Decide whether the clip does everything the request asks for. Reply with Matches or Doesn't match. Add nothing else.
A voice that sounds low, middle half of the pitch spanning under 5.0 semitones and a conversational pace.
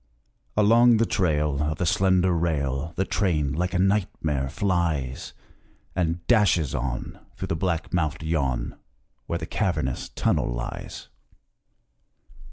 Doesn't match